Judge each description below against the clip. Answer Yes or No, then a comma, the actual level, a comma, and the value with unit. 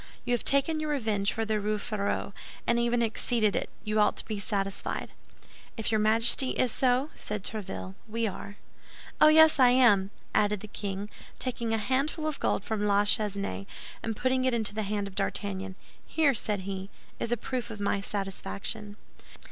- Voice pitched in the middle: No, high, 215 Hz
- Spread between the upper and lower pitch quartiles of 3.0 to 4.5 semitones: Yes, average, 3.3 semitones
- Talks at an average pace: Yes, average, 180 wpm